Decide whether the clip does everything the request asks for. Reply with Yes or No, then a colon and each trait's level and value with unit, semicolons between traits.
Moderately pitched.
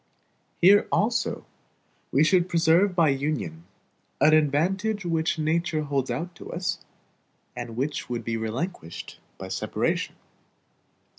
Yes: medium, 160 Hz